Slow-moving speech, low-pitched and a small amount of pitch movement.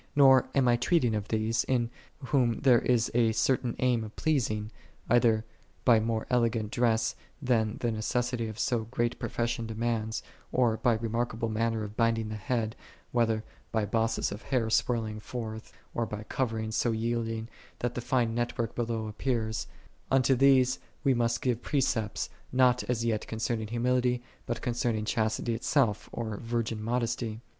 No: average, 165 wpm; low, 115 Hz; narrow, 1.8 semitones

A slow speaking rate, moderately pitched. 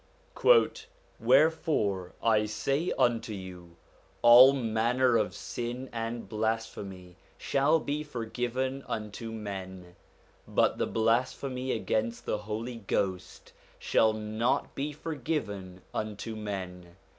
No: slow, 100 wpm; low, 115 Hz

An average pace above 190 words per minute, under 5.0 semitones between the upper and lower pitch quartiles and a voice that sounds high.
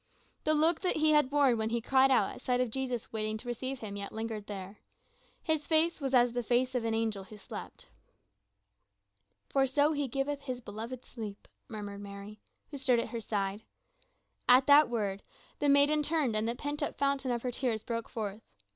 Yes: average, 200 wpm; average, 4.4 semitones; high, 245 Hz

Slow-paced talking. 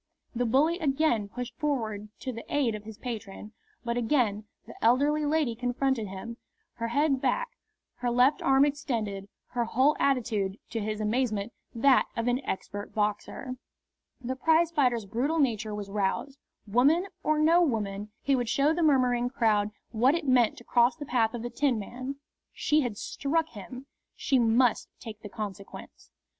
No: average, 160 wpm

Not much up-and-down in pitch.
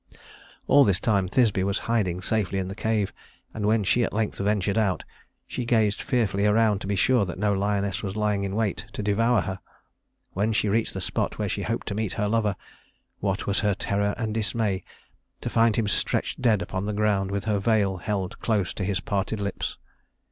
Yes: narrow, 2.0 semitones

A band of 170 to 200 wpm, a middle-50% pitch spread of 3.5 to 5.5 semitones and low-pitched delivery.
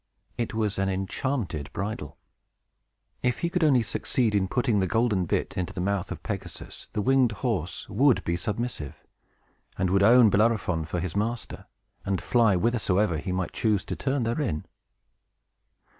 No: average, 160 wpm; average, 4.4 semitones; low, 105 Hz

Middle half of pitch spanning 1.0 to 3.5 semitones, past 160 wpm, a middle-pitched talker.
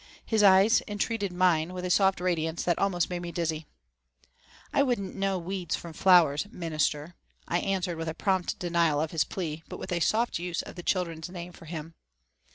Yes: average, 2.7 semitones; average, 185 wpm; medium, 175 Hz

